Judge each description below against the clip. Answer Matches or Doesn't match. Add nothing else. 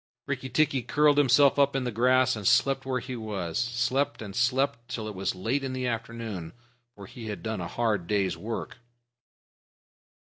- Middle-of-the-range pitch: Doesn't match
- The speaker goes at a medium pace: Matches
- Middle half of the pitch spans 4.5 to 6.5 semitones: Doesn't match